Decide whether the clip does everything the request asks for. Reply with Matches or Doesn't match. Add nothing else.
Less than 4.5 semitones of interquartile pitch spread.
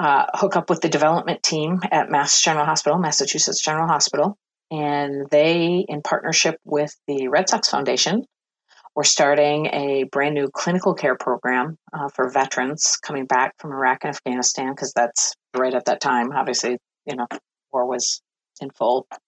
Matches